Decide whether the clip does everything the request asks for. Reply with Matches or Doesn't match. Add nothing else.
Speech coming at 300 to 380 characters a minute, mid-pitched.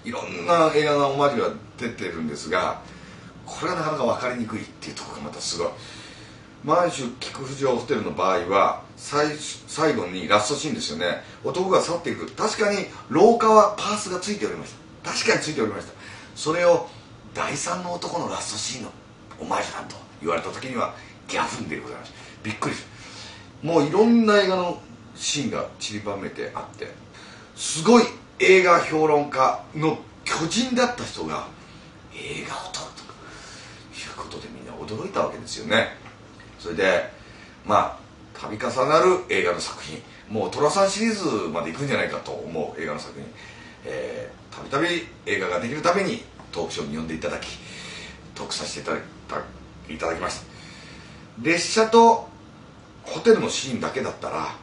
Matches